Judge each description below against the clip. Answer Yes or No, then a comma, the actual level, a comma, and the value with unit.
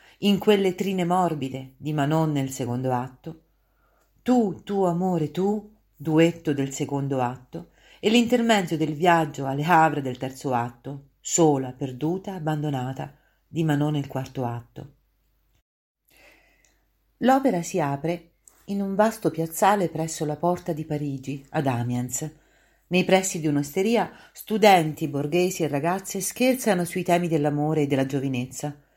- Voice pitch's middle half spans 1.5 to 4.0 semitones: No, average, 4.8 semitones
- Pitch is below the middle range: No, medium, 160 Hz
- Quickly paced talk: No, average, 130 wpm